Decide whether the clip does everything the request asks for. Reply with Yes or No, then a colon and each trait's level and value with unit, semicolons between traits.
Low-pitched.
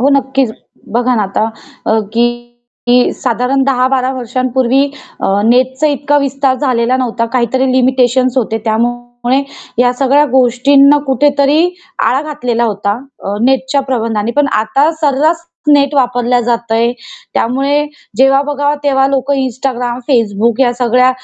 No: very high, 255 Hz